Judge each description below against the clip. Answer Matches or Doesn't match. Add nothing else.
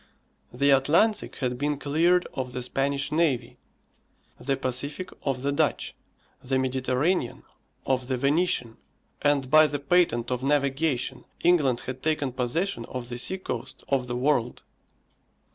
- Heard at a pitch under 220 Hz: Matches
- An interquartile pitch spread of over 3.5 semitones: Doesn't match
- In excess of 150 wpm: Doesn't match